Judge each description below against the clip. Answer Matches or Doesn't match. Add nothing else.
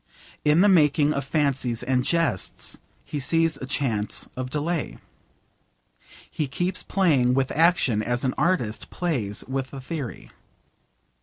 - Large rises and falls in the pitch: Doesn't match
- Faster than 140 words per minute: Doesn't match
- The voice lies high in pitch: Doesn't match